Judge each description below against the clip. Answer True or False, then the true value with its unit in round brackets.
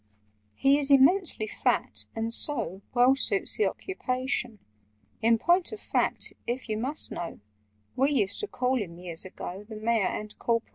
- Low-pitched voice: False (245 Hz)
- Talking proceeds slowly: False (160 wpm)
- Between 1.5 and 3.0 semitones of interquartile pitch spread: False (4.4 semitones)